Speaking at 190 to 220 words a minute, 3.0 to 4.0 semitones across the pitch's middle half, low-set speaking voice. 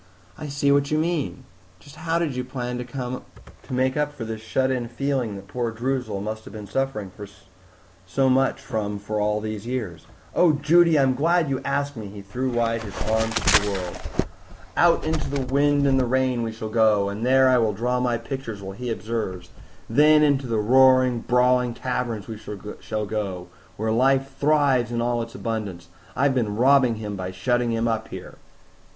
Yes: average, 195 wpm; average, 3.7 semitones; low, 125 Hz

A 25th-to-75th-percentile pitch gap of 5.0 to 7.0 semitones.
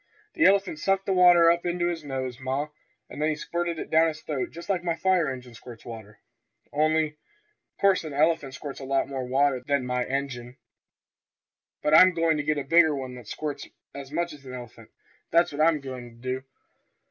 No: average, 4.3 semitones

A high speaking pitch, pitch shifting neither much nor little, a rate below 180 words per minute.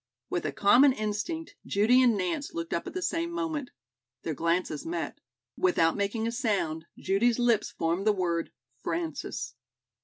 No: high, 205 Hz; wide, 6.8 semitones; average, 155 wpm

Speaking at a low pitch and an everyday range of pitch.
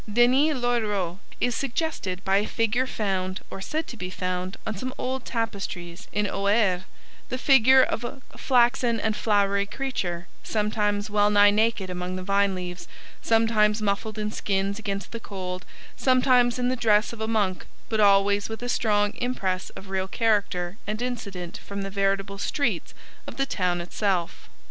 No: high, 210 Hz; average, 3.4 semitones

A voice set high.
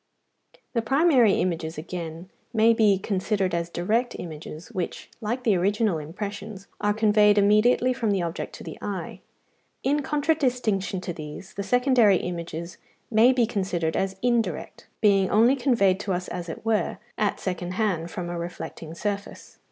Yes: high, 200 Hz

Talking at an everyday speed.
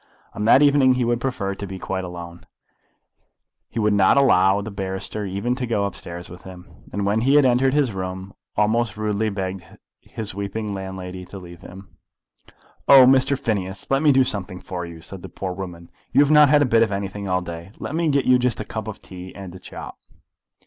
No: fast, 210 wpm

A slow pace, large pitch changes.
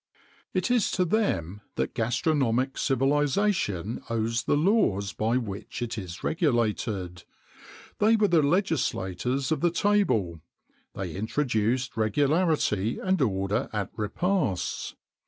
Yes: slow, 115 wpm; wide, 7.7 semitones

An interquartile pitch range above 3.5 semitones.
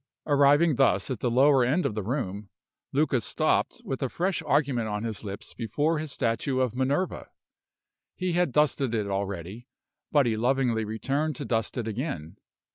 Yes: average, 4.8 semitones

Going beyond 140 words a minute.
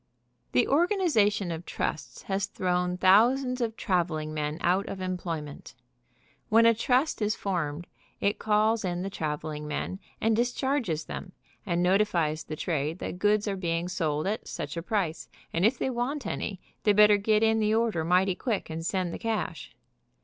Yes: average, 170 wpm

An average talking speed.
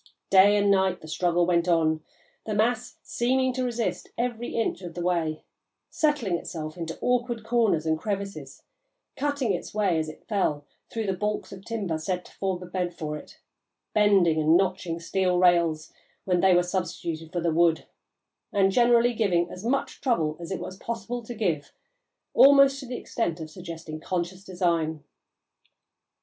Yes: average, 170 wpm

